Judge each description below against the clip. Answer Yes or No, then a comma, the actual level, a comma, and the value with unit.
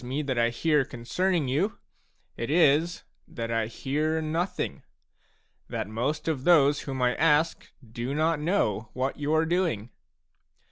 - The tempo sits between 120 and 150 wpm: Yes, average, 145 wpm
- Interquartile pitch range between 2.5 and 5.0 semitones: Yes, average, 4.7 semitones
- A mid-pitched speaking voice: Yes, medium, 145 Hz